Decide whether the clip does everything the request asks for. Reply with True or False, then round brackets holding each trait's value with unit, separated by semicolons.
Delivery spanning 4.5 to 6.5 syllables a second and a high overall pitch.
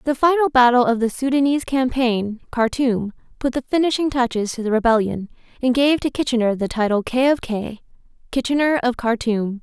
True (5.4 syllables/s; 250 Hz)